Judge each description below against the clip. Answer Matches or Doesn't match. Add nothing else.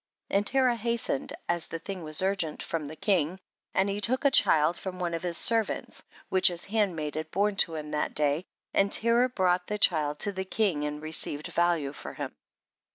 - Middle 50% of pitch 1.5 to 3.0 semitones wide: Doesn't match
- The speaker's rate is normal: Doesn't match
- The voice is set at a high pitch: Doesn't match